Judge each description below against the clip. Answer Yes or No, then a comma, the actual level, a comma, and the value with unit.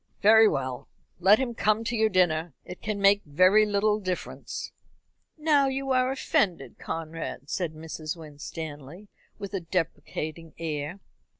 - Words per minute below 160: Yes, slow, 135 wpm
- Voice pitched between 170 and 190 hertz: Yes, medium, 185 Hz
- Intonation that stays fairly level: No, average, 5.2 semitones